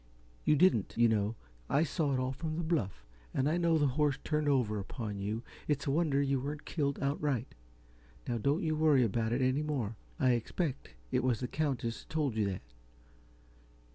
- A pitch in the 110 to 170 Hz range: Yes, low, 135 Hz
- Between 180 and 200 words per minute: Yes, average, 185 wpm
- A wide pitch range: No, average, 4.5 semitones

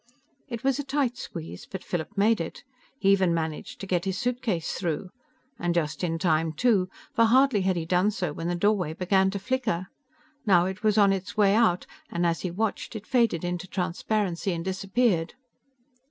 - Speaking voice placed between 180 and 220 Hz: Yes, high, 190 Hz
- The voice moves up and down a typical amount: Yes, average, 3.9 semitones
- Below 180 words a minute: No, average, 190 wpm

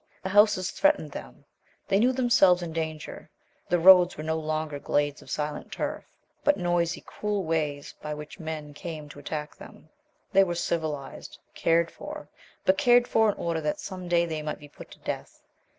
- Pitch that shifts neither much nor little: Yes, average, 3.8 semitones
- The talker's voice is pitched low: No, medium, 165 Hz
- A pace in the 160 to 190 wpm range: Yes, average, 180 wpm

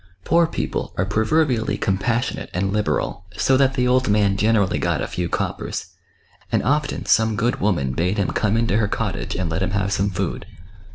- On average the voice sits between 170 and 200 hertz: No, low, 105 Hz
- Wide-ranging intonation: No, average, 3.9 semitones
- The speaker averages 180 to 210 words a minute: Yes, average, 185 wpm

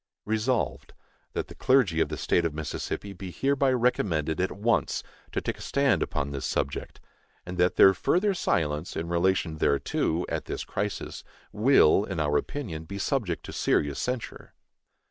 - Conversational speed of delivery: Yes, average, 165 wpm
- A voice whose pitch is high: No, very low, 95 Hz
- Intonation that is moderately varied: No, wide, 7.1 semitones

